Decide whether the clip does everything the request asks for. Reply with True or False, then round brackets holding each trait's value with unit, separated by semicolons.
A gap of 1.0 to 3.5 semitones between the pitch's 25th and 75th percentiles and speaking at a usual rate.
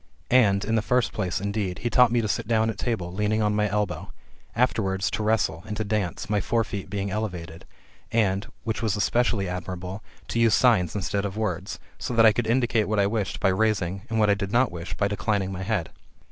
False (2.5 semitones; 220 wpm)